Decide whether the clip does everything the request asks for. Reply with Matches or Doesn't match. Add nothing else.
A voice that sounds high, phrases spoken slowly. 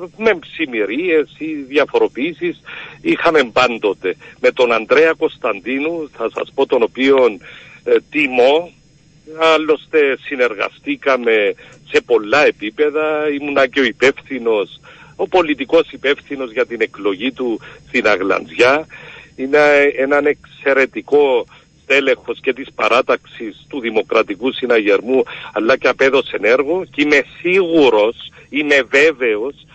Matches